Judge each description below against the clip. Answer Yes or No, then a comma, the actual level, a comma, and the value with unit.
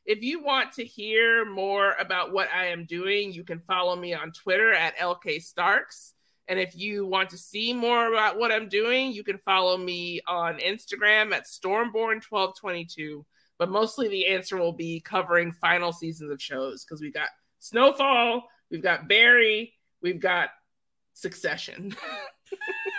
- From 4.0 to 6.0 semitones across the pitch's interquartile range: Yes, average, 4.7 semitones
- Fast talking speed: No, average, 155 wpm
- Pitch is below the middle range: No, high, 195 Hz